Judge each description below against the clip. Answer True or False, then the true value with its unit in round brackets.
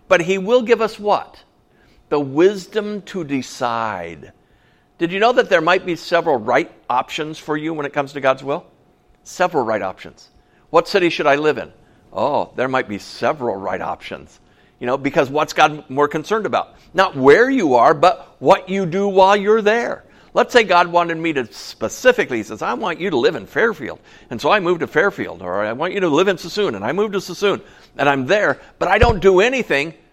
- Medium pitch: True (175 Hz)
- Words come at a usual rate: False (210 wpm)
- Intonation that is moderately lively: False (5.7 semitones)